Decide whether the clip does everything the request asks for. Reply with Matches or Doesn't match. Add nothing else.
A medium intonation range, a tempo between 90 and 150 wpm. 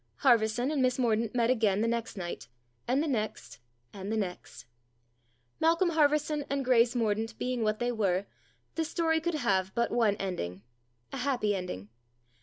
Doesn't match